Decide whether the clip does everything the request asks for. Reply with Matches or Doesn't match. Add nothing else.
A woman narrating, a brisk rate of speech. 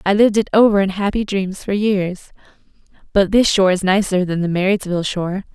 Doesn't match